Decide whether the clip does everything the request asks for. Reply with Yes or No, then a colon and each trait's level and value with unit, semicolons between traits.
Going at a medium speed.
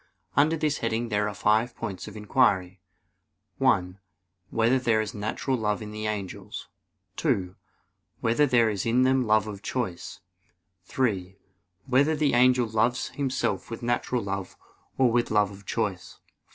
Yes: average, 150 wpm